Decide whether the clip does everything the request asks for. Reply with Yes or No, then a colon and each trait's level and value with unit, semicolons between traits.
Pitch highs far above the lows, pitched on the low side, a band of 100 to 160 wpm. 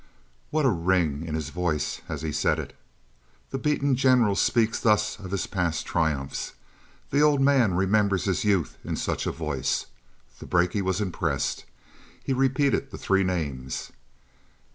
Yes: wide, 7.1 semitones; very low, 95 Hz; average, 155 wpm